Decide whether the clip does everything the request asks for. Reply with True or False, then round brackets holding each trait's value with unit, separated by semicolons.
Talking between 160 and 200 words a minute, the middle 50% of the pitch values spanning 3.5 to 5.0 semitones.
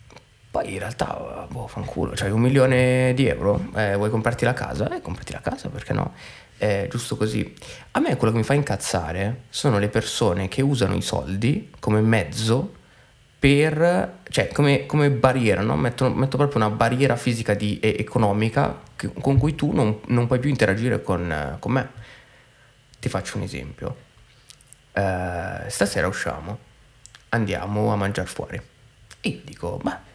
True (165 wpm; 3.9 semitones)